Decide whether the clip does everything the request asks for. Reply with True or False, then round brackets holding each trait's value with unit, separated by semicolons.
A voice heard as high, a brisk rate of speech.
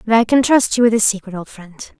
True (215 Hz; 300 wpm)